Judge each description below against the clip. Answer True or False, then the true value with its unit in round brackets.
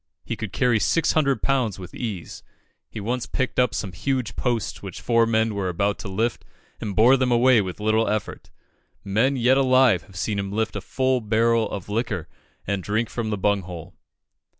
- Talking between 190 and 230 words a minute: True (195 wpm)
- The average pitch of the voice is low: True (110 Hz)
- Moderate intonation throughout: True (3.7 semitones)